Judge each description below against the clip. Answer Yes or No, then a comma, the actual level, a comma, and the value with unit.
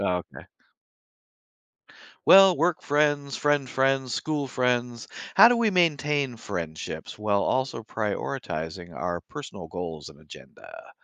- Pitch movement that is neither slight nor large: No, wide, 8.3 semitones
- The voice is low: Yes, low, 130 Hz